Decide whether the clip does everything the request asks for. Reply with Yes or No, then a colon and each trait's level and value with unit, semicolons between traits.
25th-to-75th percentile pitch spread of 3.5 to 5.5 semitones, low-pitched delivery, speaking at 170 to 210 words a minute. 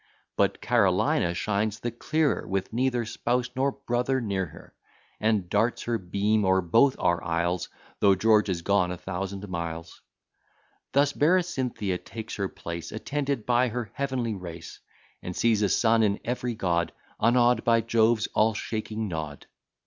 No: average, 4.5 semitones; low, 110 Hz; average, 150 wpm